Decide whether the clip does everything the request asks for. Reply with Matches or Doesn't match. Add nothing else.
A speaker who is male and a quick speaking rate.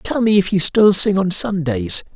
Matches